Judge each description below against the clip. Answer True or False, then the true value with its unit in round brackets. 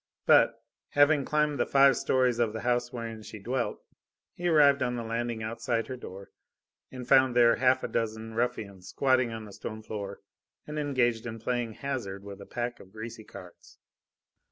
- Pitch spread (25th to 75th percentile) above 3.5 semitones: False (2.8 semitones)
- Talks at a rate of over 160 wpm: True (180 wpm)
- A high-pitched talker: False (120 Hz)